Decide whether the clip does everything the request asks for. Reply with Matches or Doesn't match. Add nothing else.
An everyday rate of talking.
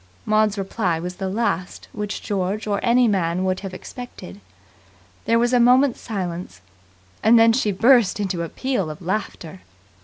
Matches